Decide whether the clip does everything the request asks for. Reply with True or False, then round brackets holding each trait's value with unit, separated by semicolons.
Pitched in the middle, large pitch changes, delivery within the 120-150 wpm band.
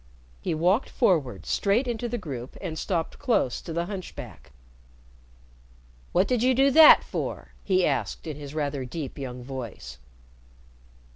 True (165 Hz; 7.8 semitones; 145 wpm)